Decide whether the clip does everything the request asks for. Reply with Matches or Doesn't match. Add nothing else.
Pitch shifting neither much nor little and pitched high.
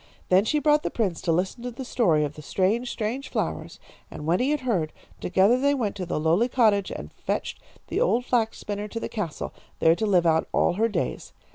Doesn't match